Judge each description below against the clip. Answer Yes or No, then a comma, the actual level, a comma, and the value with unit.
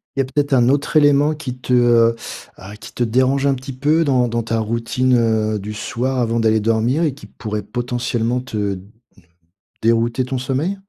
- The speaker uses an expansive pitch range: No, average, 2.8 semitones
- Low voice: Yes, low, 125 Hz